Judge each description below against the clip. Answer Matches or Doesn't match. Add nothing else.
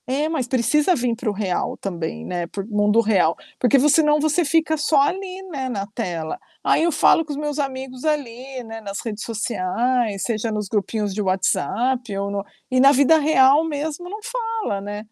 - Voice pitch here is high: Matches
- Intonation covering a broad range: Matches